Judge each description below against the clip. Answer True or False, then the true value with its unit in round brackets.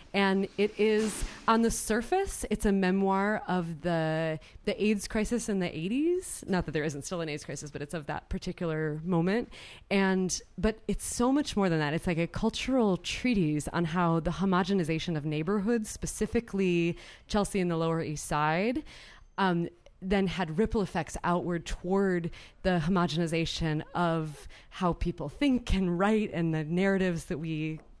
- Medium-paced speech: True (165 wpm)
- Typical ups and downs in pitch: True (4.0 semitones)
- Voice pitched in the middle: True (180 Hz)